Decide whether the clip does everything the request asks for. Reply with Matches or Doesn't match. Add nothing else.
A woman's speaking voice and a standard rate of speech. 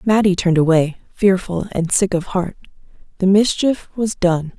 Matches